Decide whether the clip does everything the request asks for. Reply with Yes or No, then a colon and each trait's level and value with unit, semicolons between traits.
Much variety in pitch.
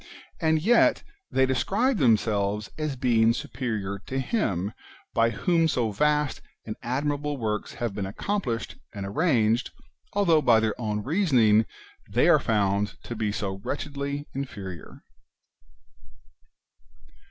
Yes: wide, 5.7 semitones